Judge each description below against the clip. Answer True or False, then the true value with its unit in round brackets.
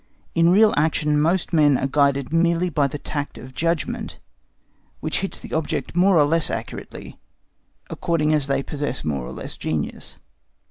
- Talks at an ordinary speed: True (165 wpm)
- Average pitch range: True (3.2 semitones)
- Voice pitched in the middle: True (150 Hz)